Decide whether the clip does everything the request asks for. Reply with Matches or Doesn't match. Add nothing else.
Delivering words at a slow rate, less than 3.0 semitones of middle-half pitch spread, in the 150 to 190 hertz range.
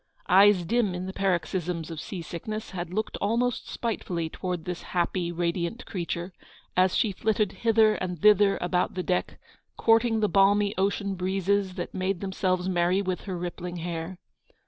Doesn't match